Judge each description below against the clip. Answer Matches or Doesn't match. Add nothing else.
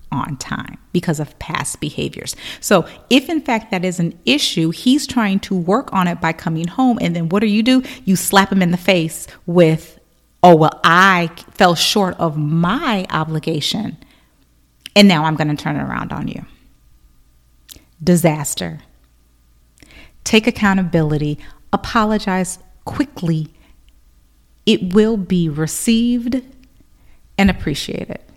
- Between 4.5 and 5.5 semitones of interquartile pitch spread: Matches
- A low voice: Doesn't match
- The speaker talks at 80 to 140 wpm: Matches